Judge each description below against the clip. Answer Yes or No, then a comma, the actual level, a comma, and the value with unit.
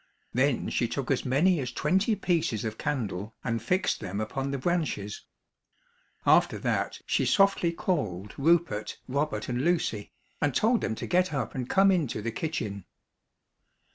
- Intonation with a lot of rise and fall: Yes, wide, 7.4 semitones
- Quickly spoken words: No, average, 155 wpm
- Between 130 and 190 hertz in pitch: Yes, low, 135 Hz